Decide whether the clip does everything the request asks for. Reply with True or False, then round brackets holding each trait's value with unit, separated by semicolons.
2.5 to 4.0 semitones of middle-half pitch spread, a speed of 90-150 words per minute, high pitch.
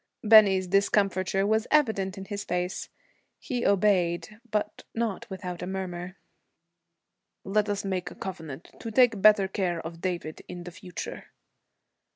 True (2.8 semitones; 140 wpm; 195 Hz)